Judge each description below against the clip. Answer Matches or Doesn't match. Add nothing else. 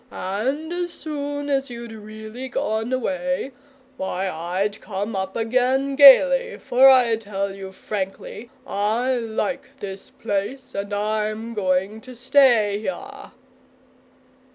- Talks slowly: Matches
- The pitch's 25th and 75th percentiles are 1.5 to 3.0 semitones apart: Doesn't match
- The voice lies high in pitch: Matches